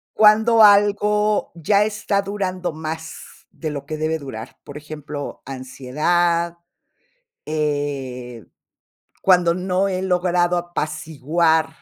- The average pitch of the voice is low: No, medium, 170 Hz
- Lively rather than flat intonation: No, average, 4.1 semitones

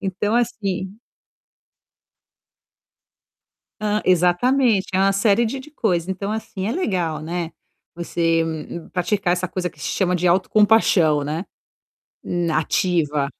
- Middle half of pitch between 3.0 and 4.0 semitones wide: Yes, average, 3.6 semitones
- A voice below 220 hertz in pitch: Yes, medium, 185 Hz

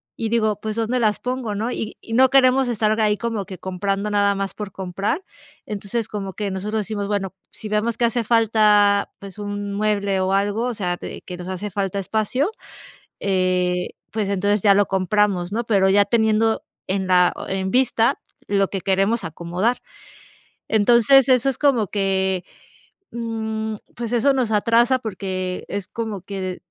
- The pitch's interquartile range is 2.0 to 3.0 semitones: Yes, average, 2.7 semitones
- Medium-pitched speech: No, high, 210 Hz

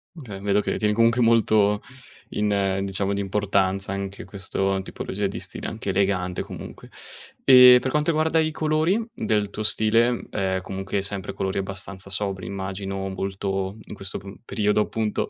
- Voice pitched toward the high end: No, low, 100 Hz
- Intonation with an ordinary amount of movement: No, narrow, 2.2 semitones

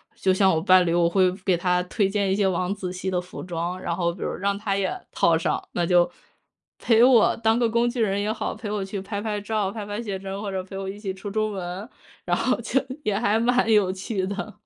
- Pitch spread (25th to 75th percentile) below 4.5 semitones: Yes, narrow, 2.6 semitones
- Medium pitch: No, high, 195 Hz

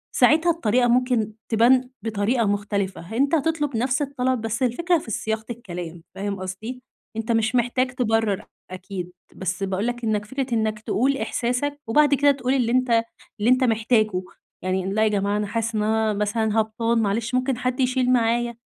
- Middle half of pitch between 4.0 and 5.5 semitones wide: No, average, 3.2 semitones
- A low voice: No, high, 230 Hz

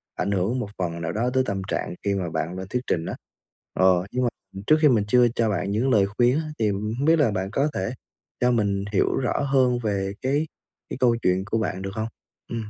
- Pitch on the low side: Yes, low, 105 Hz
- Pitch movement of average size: Yes, average, 4.4 semitones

